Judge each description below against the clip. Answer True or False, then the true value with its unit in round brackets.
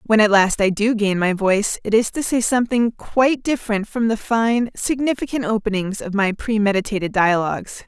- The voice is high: True (220 Hz)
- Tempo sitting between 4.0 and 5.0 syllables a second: False (5.3 syllables/s)